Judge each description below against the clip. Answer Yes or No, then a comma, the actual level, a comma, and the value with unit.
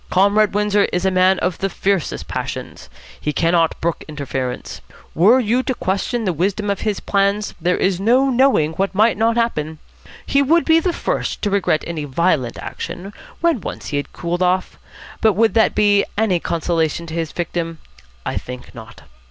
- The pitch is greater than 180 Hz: Yes, high, 190 Hz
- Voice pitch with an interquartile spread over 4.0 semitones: Yes, average, 4.5 semitones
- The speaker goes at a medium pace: Yes, average, 180 wpm